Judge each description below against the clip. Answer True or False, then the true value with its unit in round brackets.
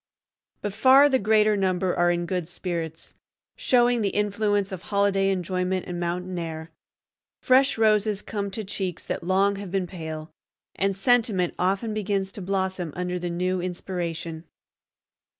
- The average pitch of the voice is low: False (190 Hz)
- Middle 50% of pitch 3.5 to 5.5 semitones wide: False (2.6 semitones)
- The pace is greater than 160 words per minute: False (150 wpm)